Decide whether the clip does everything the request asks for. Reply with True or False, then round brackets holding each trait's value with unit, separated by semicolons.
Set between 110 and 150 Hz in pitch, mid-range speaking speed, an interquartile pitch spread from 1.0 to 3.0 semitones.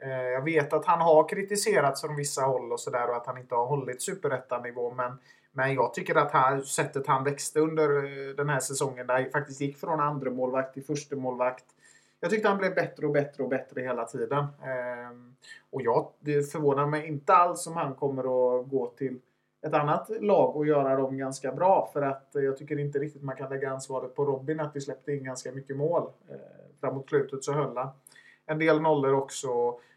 False (140 Hz; 205 wpm; 2.6 semitones)